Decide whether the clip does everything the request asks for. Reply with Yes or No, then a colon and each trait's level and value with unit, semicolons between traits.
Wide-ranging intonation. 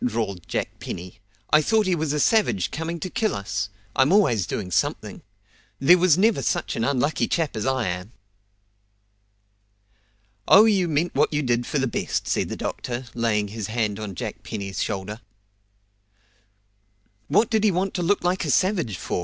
Yes: wide, 9.0 semitones